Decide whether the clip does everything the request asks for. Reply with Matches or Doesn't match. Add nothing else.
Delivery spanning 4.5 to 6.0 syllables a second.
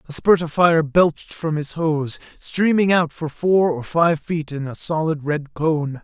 Doesn't match